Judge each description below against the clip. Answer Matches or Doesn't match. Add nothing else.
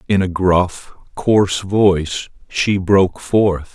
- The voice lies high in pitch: Doesn't match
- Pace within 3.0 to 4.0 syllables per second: Matches